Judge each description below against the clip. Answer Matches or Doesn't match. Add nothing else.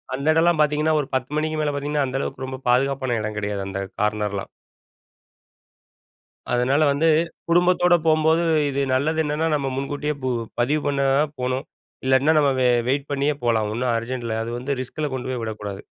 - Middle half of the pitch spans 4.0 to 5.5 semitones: Doesn't match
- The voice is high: Doesn't match